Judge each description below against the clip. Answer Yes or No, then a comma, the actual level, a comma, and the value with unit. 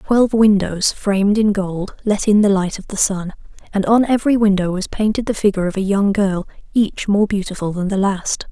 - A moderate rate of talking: No, fast, 210 wpm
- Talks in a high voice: Yes, high, 200 Hz